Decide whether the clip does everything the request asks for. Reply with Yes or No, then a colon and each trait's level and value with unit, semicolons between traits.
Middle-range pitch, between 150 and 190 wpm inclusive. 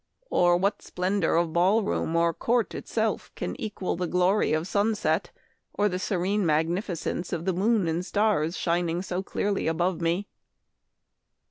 Yes: medium, 180 Hz; average, 155 wpm